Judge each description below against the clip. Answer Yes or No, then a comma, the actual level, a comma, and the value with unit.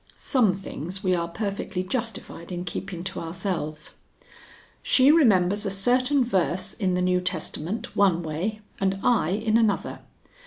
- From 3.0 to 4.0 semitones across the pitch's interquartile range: Yes, average, 3.5 semitones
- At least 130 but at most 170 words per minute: Yes, average, 145 wpm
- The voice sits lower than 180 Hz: No, high, 190 Hz